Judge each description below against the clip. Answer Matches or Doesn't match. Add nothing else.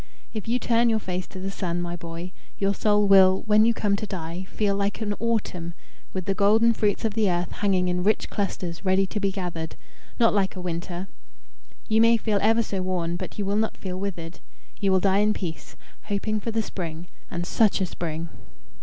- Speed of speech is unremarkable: Doesn't match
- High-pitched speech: Matches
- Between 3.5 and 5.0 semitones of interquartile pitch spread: Doesn't match